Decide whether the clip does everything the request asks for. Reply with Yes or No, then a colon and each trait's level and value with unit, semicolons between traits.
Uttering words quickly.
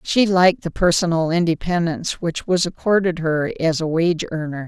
No: average, 165 wpm